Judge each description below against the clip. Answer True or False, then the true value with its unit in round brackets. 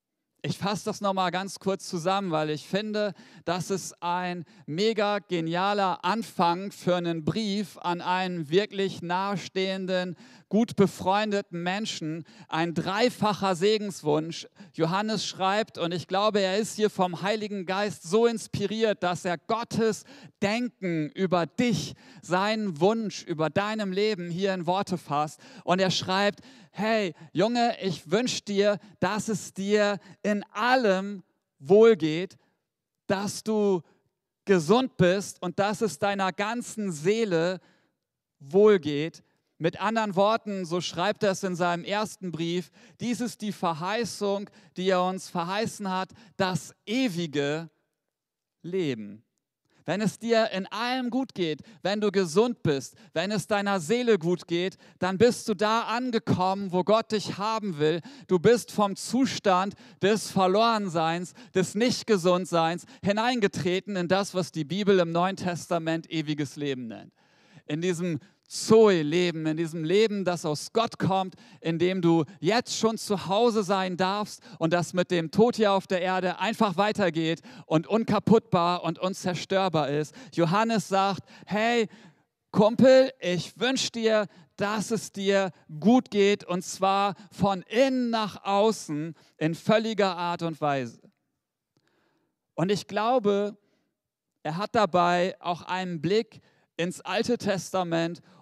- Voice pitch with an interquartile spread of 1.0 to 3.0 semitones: False (3.5 semitones)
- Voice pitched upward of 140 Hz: True (190 Hz)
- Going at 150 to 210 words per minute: False (135 wpm)